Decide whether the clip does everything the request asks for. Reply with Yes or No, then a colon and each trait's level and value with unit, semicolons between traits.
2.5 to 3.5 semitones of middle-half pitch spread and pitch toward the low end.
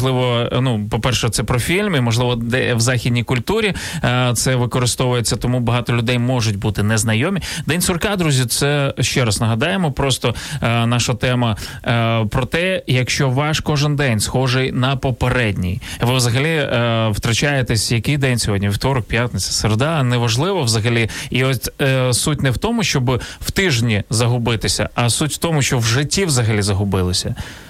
Yes: average, 2.9 semitones; low, 125 Hz